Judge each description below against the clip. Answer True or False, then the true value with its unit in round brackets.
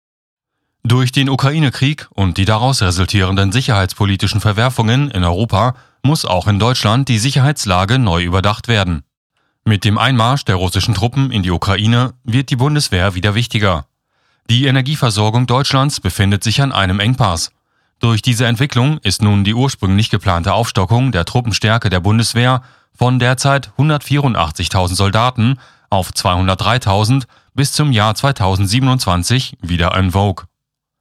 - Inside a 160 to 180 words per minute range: False (130 wpm)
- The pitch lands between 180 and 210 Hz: False (115 Hz)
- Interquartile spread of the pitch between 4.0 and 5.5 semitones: True (4.7 semitones)